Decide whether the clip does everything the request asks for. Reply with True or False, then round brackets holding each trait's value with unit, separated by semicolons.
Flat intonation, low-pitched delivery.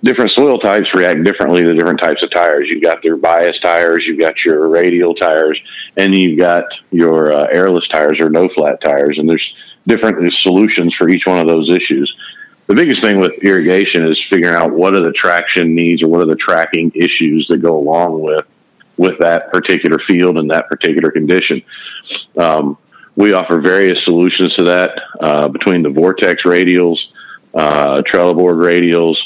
True (1.6 semitones; 85 Hz)